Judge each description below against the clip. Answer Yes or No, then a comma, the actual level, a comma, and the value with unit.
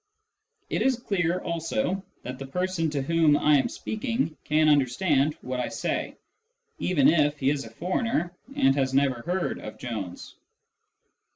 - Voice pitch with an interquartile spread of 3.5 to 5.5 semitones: Yes, average, 5.1 semitones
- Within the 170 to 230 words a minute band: No, average, 155 wpm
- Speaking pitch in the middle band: Yes, medium, 150 Hz